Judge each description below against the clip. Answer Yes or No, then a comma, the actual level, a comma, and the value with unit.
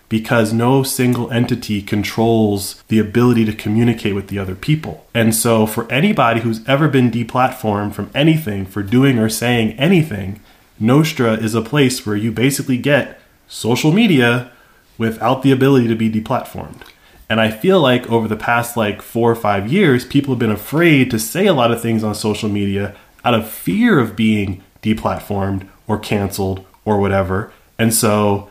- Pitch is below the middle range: Yes, low, 115 Hz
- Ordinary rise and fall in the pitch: Yes, average, 3.3 semitones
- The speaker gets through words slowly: No, average, 170 wpm